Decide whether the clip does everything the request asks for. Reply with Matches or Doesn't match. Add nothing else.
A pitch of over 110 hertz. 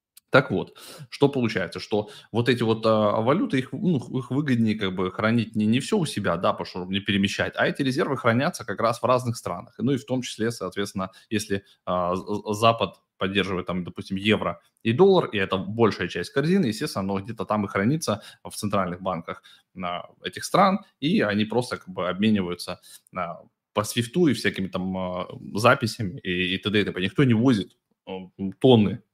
Doesn't match